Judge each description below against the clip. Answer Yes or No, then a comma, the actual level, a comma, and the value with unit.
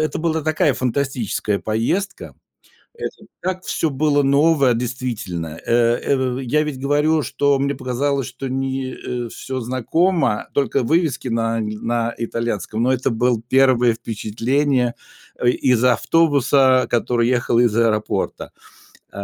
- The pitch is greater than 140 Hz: No, low, 130 Hz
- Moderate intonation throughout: Yes, average, 3.3 semitones